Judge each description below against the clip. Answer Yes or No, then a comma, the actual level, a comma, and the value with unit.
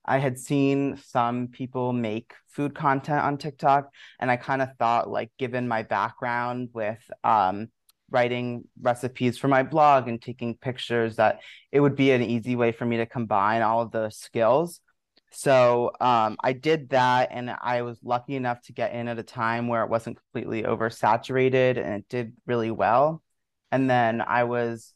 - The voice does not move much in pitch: Yes, narrow, 2.1 semitones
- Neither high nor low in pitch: No, low, 120 Hz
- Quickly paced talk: No, average, 180 wpm